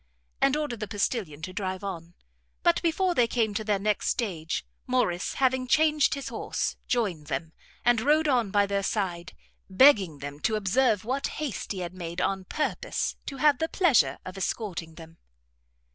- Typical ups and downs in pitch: No, wide, 6.3 semitones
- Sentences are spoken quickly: No, average, 175 wpm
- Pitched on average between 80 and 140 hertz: No, high, 210 Hz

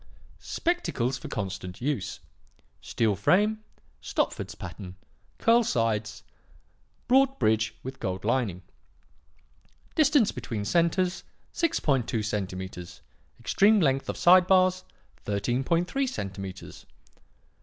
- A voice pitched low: Yes, low, 125 Hz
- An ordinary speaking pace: No, slow, 90 wpm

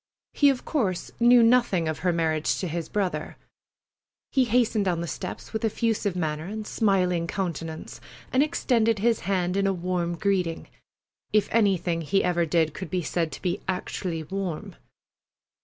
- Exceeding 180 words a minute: No, average, 155 wpm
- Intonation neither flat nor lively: Yes, average, 4.3 semitones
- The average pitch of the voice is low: No, medium, 185 Hz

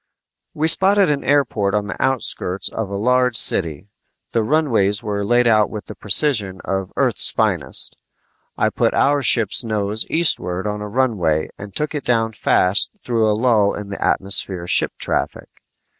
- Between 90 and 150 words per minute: No, average, 165 wpm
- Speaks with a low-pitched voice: Yes, low, 110 Hz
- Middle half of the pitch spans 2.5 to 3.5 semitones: No, average, 4.1 semitones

